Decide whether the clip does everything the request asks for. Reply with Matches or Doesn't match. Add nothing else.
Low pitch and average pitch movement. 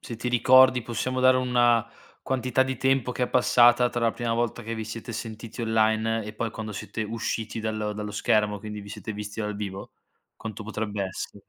Doesn't match